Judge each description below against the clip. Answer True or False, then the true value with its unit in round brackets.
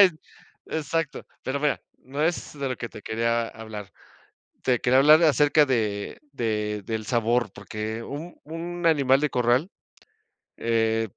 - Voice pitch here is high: False (125 Hz)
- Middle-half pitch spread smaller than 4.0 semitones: False (4.9 semitones)